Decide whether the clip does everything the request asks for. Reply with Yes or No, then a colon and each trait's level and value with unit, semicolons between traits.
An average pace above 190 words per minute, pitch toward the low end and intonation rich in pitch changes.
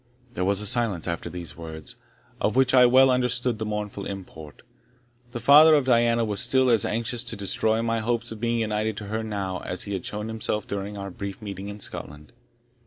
No: fast, 205 wpm; low, 110 Hz; average, 3.1 semitones